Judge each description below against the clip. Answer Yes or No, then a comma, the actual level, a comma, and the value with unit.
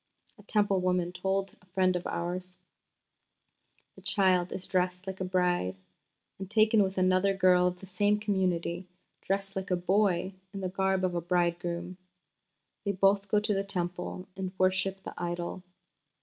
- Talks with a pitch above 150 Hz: Yes, medium, 185 Hz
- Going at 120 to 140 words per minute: No, average, 165 wpm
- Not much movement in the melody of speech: Yes, narrow, 1.5 semitones